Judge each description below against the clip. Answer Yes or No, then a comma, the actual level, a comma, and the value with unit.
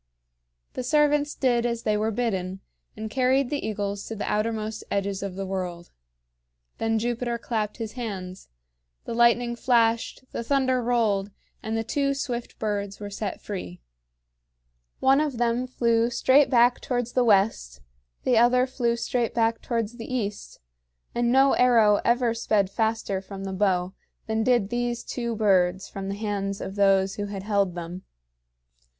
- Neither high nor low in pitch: No, high, 225 Hz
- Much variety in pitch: No, average, 3.3 semitones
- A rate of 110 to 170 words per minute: Yes, average, 160 wpm